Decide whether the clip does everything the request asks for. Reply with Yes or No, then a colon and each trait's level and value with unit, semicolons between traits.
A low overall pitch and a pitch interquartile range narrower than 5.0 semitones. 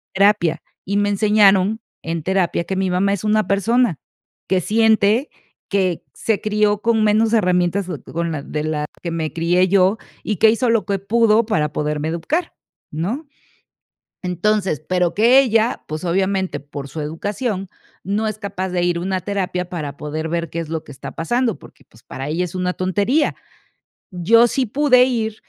No: high, 190 Hz; average, 4.1 semitones